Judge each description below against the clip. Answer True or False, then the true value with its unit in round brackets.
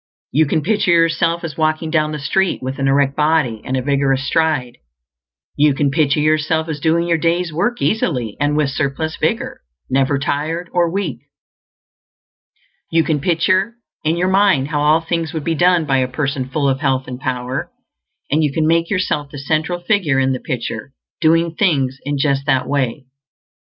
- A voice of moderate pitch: True (150 Hz)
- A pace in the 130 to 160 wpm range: False (185 wpm)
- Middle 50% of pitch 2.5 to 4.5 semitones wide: True (3.3 semitones)